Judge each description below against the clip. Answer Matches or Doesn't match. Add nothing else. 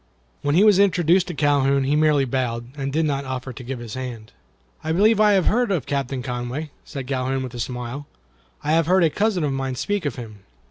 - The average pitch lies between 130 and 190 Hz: Matches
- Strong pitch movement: Doesn't match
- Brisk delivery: Matches